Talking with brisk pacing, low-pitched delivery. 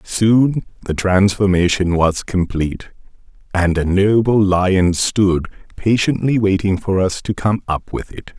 No: slow, 135 wpm; very low, 95 Hz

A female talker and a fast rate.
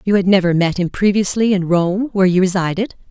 Yes: female; fast, 210 wpm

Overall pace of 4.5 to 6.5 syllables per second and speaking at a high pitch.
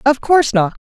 Yes: 5.8 syllables/s; very high, 260 Hz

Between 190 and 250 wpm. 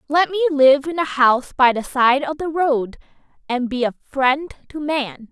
Yes: fast, 205 wpm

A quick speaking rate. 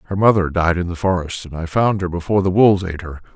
Yes: fast, 270 wpm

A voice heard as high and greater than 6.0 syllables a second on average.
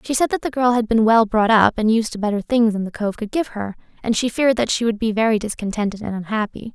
Yes: high, 220 Hz; 6.3 syllables/s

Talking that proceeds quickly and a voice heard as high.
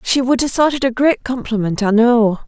Yes: fast, 245 wpm; high, 240 Hz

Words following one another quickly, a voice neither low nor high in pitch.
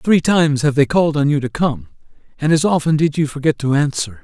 Yes: fast, 240 wpm; medium, 145 Hz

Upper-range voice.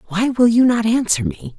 Yes: high, 215 Hz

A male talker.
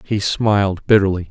Yes: male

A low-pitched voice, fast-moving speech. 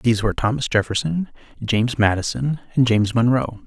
No: low, 120 Hz; average, 145 wpm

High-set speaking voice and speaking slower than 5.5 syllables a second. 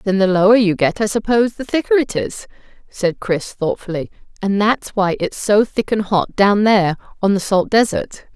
Yes: high, 205 Hz; 5.0 syllables/s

